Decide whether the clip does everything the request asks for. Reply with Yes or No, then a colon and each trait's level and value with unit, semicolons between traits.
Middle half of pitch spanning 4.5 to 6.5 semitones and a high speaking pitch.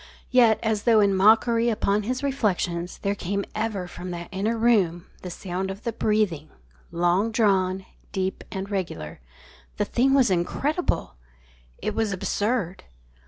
No: average, 3.5 semitones; high, 200 Hz